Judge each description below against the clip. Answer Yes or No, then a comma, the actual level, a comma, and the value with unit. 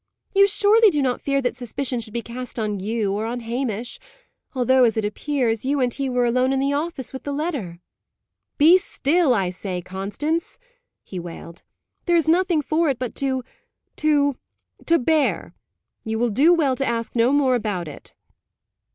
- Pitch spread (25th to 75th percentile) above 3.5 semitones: Yes, average, 4.6 semitones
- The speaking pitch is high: Yes, very high, 255 Hz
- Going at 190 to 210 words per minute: No, average, 180 wpm